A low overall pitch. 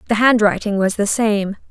No: high, 210 Hz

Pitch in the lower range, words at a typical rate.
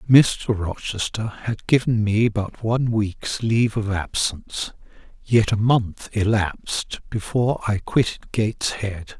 No: low, 110 Hz; slow, 125 wpm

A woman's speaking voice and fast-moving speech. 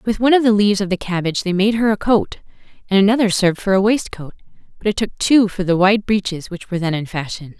Yes: female; fast, 255 wpm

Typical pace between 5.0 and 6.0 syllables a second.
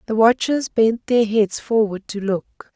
No: 3.9 syllables/s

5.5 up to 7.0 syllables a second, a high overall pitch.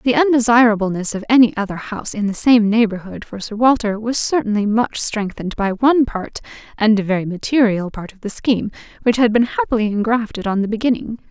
Yes: 5.9 syllables/s; high, 220 Hz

